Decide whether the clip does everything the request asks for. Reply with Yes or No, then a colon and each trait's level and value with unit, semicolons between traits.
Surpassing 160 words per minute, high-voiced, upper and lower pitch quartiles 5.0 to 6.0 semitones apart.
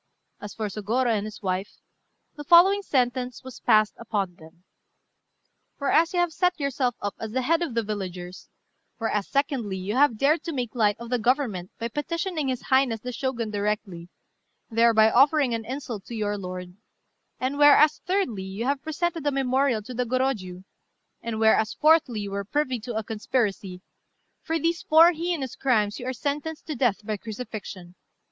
Yes: average, 175 wpm; high, 240 Hz; average, 5.3 semitones